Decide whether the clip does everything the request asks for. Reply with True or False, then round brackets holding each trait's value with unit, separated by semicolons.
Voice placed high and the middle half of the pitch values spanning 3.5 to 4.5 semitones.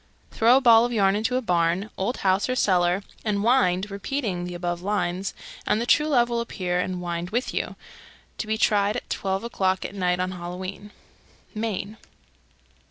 True (200 Hz; 4.0 semitones)